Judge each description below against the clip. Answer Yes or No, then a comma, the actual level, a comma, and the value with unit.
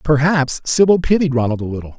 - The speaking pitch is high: No, medium, 140 Hz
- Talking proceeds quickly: No, average, 180 wpm